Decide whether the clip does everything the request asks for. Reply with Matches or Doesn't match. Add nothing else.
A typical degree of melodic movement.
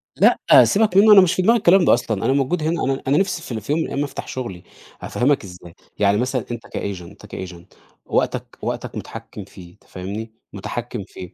Doesn't match